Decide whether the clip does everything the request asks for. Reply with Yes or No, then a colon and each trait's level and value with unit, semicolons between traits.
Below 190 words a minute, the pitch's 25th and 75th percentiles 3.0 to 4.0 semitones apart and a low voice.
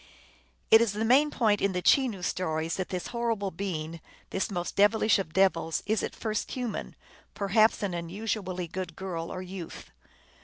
No: average, 165 wpm; average, 3.6 semitones; high, 195 Hz